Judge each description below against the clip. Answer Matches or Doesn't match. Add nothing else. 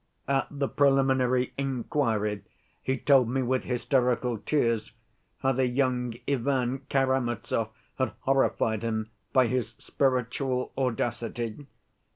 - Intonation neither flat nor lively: Doesn't match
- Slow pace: Matches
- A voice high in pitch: Doesn't match